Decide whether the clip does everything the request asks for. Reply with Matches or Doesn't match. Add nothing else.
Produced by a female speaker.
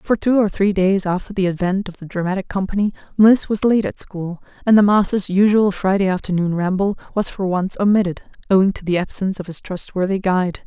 Matches